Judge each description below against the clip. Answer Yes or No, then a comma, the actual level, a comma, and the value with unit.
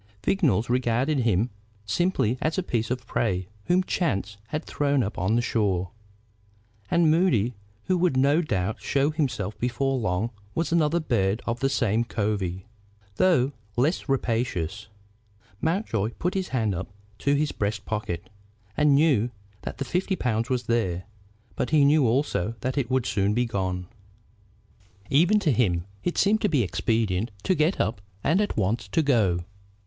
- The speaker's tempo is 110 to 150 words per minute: No, average, 160 wpm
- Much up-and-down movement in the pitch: Yes, wide, 6.4 semitones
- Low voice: Yes, low, 120 Hz